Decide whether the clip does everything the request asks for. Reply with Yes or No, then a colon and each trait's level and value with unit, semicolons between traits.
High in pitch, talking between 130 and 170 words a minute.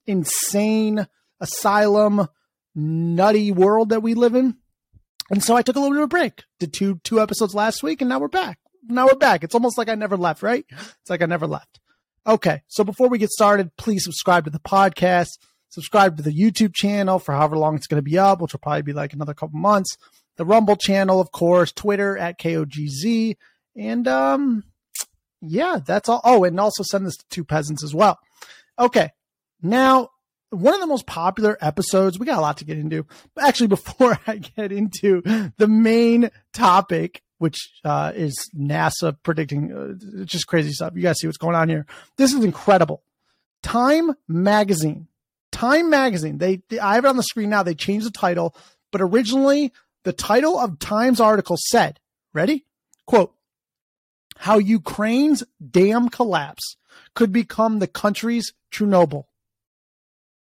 No: high, 200 Hz; average, 180 wpm